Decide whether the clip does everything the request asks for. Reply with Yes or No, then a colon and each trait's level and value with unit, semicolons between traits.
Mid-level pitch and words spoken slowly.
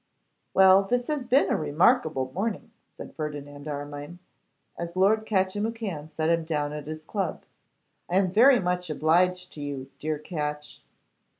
No: medium, 170 Hz; average, 145 wpm